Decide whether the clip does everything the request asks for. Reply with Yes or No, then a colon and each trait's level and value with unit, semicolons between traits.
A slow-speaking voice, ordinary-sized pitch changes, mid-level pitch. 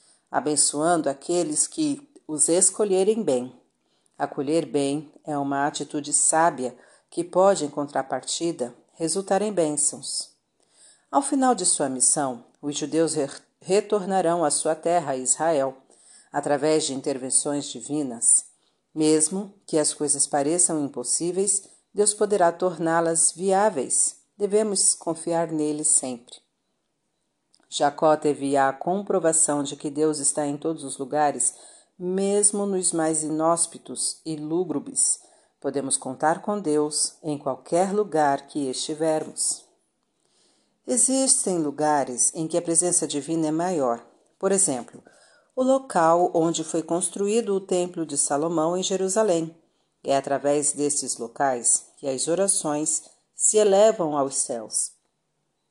Yes: slow, 115 wpm; average, 4.0 semitones; medium, 155 Hz